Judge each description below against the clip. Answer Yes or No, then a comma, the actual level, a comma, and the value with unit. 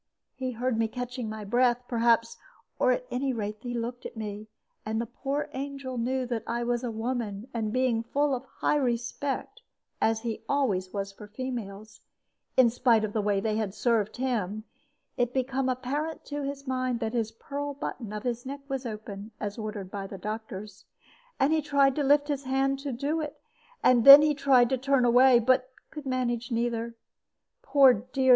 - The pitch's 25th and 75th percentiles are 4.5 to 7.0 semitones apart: No, average, 3.3 semitones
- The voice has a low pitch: No, high, 245 Hz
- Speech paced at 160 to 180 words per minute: No, average, 190 wpm